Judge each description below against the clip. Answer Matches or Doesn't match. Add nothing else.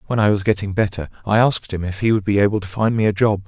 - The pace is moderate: Doesn't match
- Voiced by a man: Matches